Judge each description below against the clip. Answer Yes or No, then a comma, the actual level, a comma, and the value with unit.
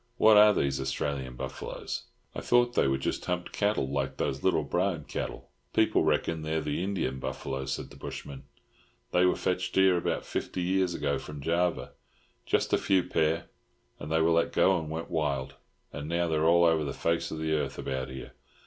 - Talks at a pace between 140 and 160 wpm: No, average, 190 wpm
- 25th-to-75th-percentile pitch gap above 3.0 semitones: Yes, average, 4.0 semitones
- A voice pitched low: Yes, very low, 80 Hz